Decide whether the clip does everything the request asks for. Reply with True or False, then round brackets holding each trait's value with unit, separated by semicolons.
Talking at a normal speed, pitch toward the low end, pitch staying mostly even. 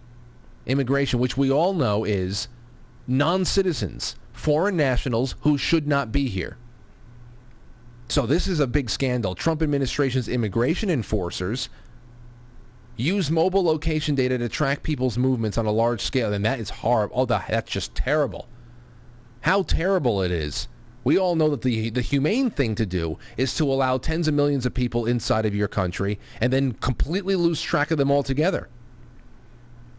False (155 wpm; 125 Hz; 3.6 semitones)